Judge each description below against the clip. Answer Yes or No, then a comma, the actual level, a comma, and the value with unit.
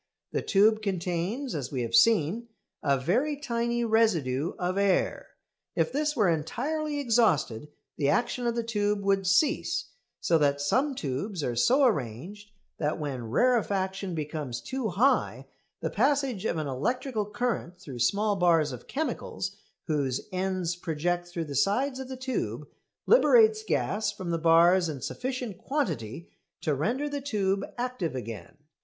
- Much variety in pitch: Yes, wide, 8.0 semitones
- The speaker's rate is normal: Yes, average, 150 wpm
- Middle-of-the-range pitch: No, high, 195 Hz